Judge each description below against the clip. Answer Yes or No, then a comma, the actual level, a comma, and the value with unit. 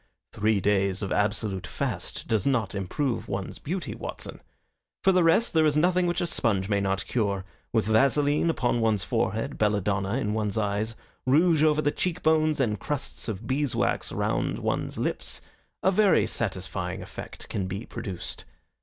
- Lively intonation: Yes, wide, 7.2 semitones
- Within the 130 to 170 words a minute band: Yes, average, 165 wpm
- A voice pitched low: Yes, low, 110 Hz